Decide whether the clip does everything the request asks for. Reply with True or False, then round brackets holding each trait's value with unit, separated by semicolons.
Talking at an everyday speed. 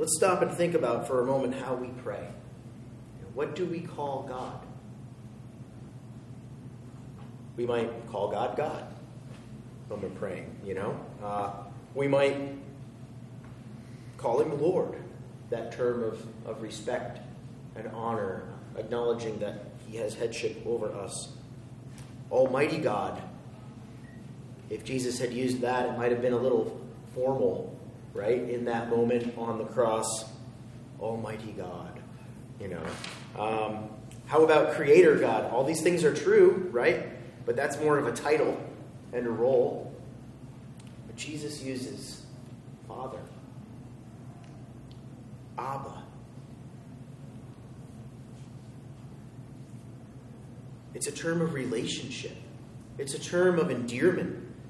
False (115 wpm)